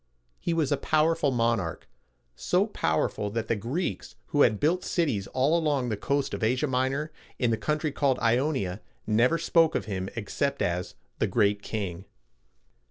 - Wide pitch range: Yes, wide, 6.1 semitones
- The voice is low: Yes, low, 130 Hz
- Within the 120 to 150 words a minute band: No, average, 165 wpm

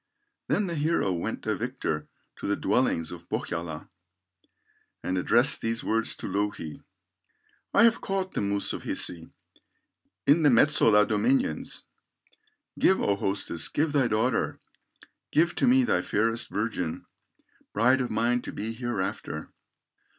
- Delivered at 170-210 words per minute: No, slow, 135 wpm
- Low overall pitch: Yes, low, 115 Hz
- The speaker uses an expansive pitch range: Yes, wide, 6.7 semitones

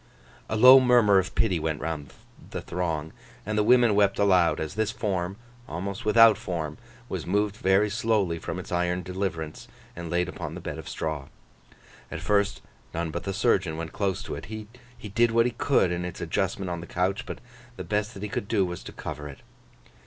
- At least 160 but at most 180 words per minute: No, average, 200 wpm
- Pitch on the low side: Yes, very low, 95 Hz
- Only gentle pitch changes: No, average, 3.7 semitones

